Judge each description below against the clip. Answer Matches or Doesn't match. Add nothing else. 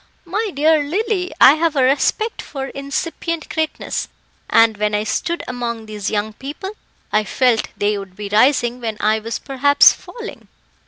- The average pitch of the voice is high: Matches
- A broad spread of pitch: Matches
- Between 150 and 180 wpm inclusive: Matches